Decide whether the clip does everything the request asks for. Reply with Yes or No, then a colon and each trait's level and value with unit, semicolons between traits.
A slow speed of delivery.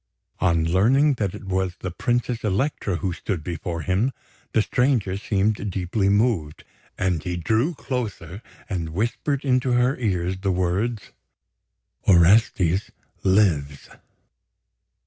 Yes: slow, 120 wpm